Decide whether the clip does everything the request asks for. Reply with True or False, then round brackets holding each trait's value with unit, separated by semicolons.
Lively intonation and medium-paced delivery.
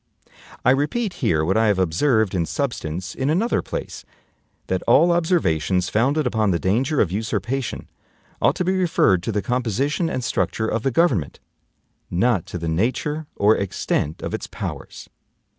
True (7.4 semitones; 160 wpm)